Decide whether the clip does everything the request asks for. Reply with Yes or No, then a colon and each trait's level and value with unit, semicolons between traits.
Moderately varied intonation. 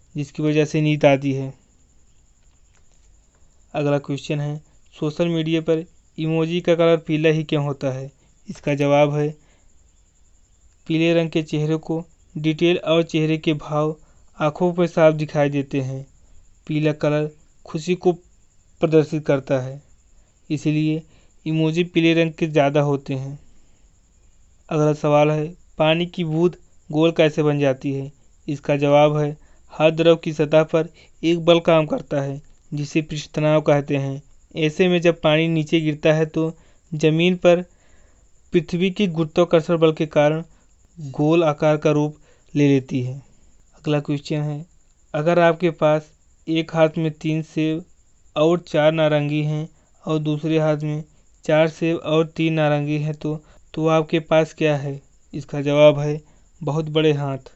No: narrow, 2.0 semitones